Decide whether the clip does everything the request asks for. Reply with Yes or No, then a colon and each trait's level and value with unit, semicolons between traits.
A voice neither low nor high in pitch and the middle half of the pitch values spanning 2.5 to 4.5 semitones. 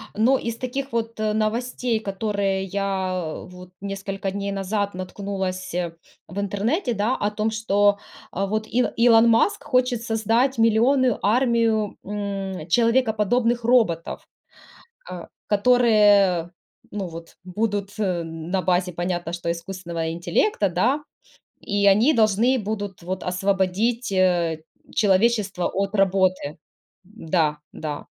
No: high, 200 Hz; average, 3.5 semitones